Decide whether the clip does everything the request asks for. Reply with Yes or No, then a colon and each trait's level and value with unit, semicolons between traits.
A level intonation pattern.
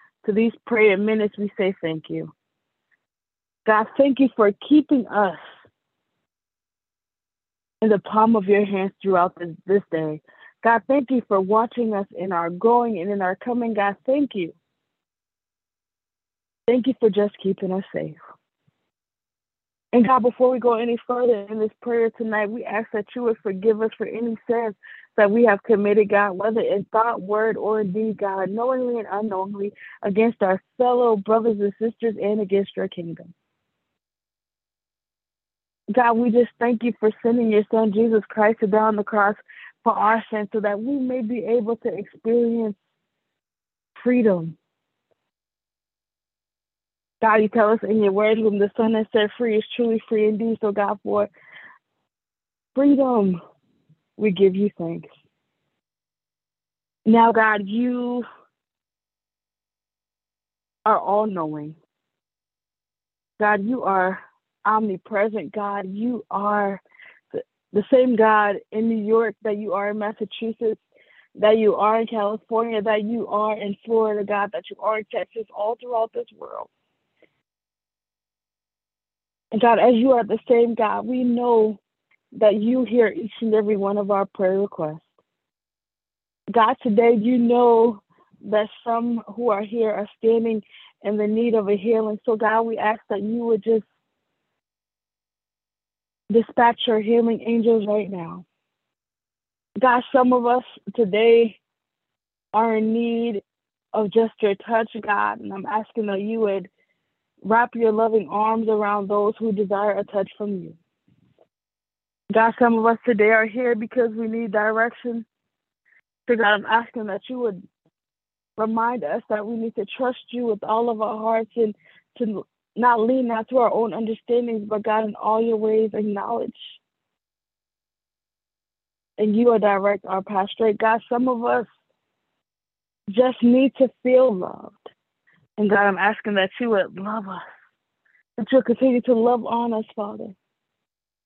Yes: narrow, 2.3 semitones